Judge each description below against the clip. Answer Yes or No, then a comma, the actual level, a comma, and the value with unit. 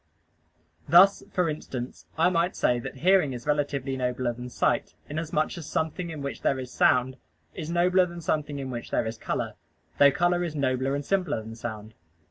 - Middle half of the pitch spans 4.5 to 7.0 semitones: Yes, average, 5.0 semitones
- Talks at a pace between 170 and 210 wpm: Yes, average, 185 wpm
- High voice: No, medium, 145 Hz